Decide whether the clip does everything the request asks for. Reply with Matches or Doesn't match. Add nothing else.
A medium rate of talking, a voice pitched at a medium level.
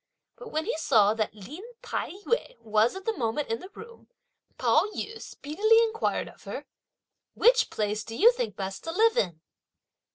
Doesn't match